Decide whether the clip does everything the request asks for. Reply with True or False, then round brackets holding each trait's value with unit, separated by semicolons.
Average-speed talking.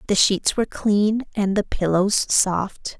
True (160 wpm)